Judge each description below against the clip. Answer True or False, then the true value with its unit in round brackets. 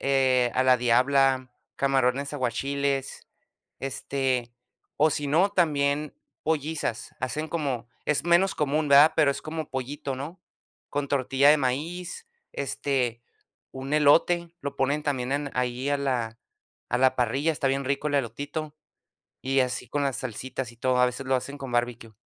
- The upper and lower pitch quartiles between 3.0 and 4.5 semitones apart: False (2.4 semitones)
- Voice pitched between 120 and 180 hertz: True (140 Hz)